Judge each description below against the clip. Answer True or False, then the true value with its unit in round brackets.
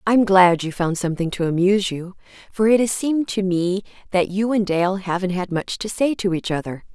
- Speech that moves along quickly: True (225 wpm)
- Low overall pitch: False (190 Hz)